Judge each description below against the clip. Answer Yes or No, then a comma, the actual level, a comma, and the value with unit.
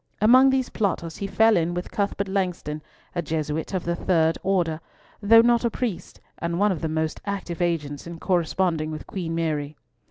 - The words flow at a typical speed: Yes, average, 185 wpm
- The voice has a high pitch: No, medium, 175 Hz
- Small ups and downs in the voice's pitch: No, average, 3.8 semitones